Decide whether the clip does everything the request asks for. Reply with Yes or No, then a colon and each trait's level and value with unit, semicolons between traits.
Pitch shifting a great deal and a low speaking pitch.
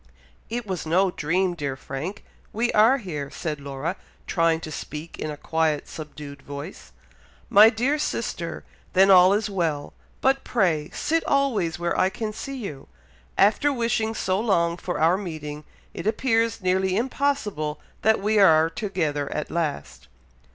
No: wide, 6.0 semitones; medium, 185 Hz